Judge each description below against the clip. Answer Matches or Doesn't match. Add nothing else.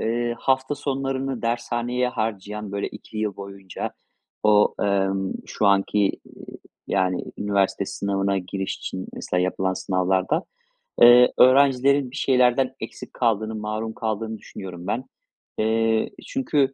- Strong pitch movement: Doesn't match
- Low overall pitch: Matches